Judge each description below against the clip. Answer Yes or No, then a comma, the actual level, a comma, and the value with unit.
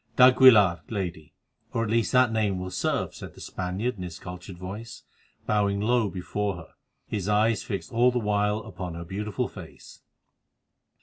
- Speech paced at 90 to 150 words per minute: No, average, 165 wpm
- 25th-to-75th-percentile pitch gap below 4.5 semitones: Yes, average, 3.5 semitones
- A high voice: No, low, 105 Hz